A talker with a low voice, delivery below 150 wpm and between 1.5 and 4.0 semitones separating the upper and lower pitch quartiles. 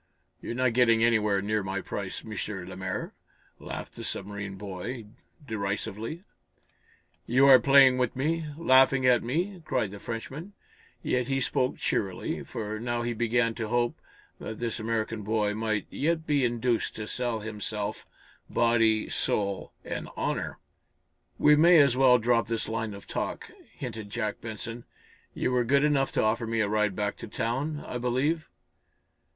No: low, 115 Hz; average, 155 wpm; average, 3.2 semitones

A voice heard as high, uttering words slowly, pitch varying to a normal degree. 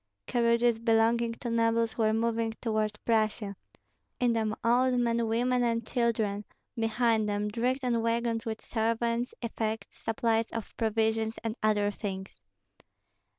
No: high, 230 Hz; slow, 130 wpm; narrow, 1.2 semitones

